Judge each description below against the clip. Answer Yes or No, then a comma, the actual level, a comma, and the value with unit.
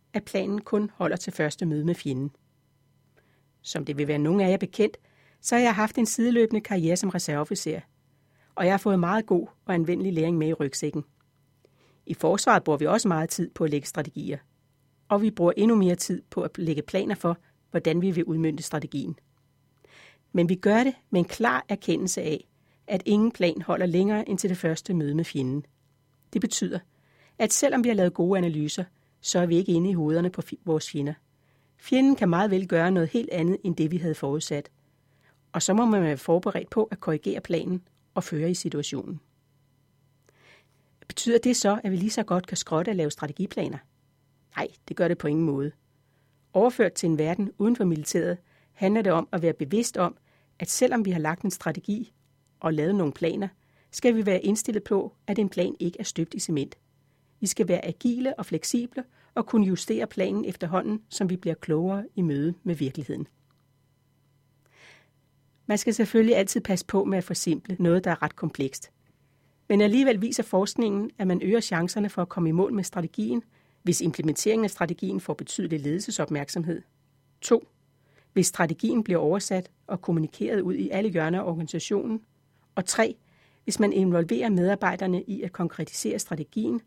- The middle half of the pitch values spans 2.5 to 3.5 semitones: No, average, 5.3 semitones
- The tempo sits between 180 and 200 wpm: Yes, average, 185 wpm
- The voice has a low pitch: No, medium, 170 Hz